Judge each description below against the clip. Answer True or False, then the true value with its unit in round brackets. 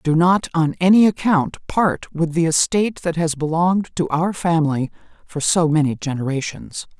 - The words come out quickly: False (165 wpm)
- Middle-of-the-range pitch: True (165 Hz)